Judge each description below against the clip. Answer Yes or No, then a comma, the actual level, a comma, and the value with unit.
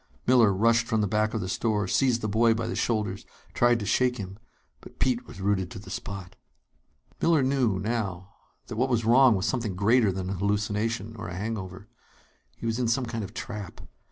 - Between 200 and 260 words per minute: Yes, fast, 205 wpm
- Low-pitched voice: Yes, low, 110 Hz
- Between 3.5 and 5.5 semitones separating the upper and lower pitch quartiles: No, average, 3.1 semitones